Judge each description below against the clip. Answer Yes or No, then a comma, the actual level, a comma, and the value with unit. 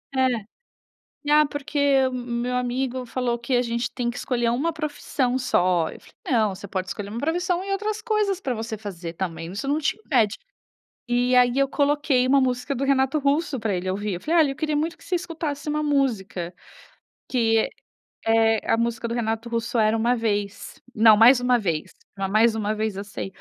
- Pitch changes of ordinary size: Yes, average, 4.3 semitones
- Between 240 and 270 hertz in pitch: Yes, high, 245 Hz